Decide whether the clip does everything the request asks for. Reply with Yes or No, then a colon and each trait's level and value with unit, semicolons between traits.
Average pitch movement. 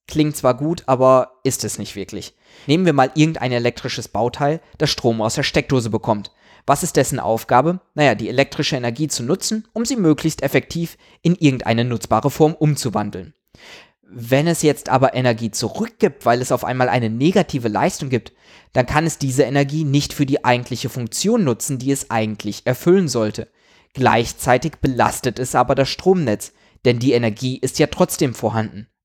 Yes: average, 4.5 semitones